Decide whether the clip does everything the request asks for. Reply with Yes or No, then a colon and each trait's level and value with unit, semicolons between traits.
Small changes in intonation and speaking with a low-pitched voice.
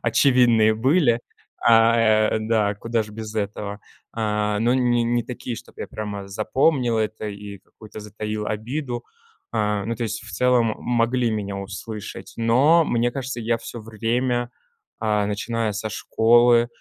Yes: narrow, 2.2 semitones; low, 115 Hz